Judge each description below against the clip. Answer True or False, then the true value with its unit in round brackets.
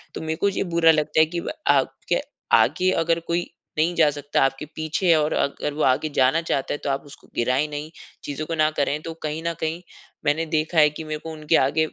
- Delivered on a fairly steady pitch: True (1.8 semitones)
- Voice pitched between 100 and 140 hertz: False (155 Hz)